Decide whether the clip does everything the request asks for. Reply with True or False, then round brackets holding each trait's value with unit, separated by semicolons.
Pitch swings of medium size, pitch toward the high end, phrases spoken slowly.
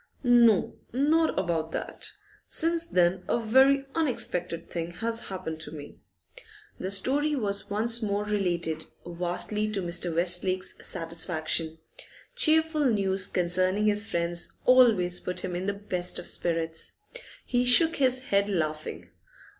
False (5.8 semitones; 195 Hz; 130 wpm)